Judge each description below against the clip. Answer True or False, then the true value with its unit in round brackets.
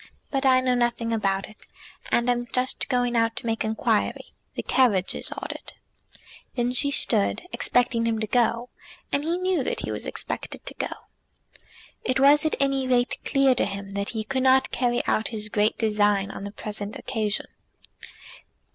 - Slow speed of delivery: False (175 wpm)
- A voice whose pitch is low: False (240 Hz)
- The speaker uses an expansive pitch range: False (3.3 semitones)